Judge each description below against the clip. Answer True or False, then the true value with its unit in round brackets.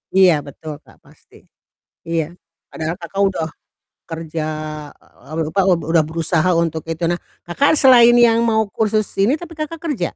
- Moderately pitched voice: True (175 Hz)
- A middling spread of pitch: False (6.0 semitones)